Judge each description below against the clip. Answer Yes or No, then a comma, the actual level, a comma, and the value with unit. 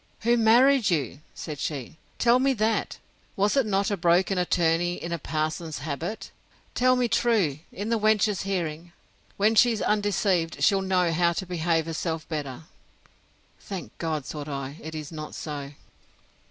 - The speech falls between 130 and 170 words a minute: Yes, average, 155 wpm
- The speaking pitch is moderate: Yes, medium, 175 Hz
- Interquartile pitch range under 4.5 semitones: No, average, 5.1 semitones